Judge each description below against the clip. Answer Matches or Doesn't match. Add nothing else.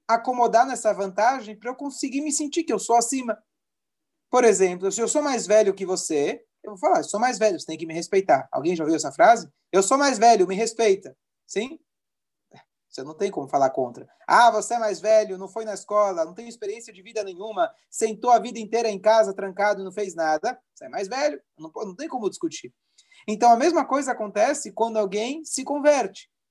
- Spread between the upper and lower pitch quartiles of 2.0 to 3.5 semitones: Doesn't match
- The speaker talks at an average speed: Doesn't match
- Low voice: Doesn't match